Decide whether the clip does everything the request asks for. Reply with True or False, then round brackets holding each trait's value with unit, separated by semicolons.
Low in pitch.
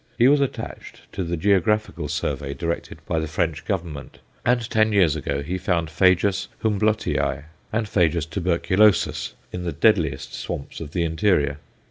True (90 Hz)